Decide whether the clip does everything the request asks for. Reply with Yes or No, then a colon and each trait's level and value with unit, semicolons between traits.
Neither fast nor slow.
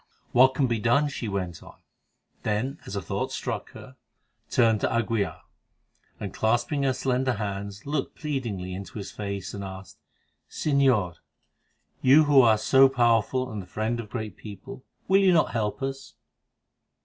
Yes: average, 160 wpm